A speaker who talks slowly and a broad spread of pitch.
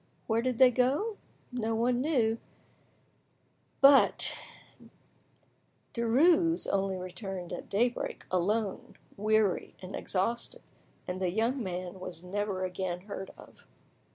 No: slow, 110 wpm; average, 4.8 semitones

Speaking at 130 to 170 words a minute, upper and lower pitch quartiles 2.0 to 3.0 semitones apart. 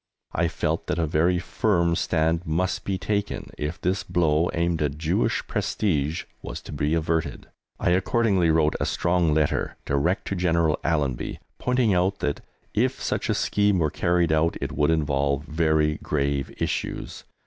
Yes: average, 160 wpm; average, 2.7 semitones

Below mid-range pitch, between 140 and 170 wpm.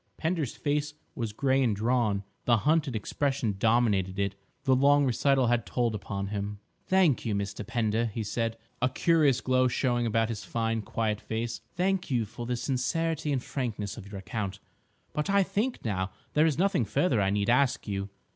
No: low, 120 Hz; average, 180 wpm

